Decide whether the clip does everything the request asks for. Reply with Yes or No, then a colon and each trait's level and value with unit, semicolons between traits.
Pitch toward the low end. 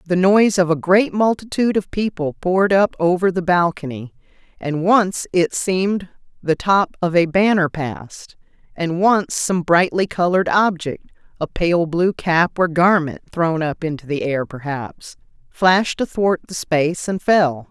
No: medium, 175 Hz